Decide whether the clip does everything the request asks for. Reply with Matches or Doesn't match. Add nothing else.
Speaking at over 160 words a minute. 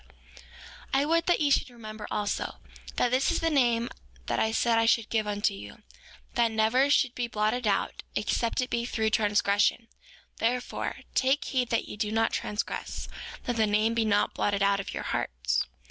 Matches